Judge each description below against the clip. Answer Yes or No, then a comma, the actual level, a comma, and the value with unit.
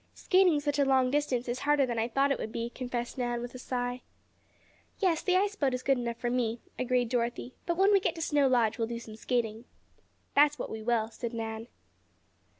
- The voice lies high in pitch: Yes, very high, 250 Hz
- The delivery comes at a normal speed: No, fast, 220 wpm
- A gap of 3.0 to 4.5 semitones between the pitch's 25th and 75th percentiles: Yes, average, 3.3 semitones